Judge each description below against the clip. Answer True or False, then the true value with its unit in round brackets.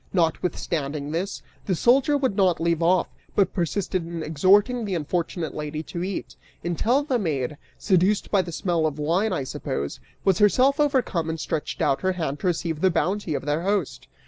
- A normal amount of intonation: True (4.1 semitones)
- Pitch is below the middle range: False (175 Hz)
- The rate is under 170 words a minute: False (185 wpm)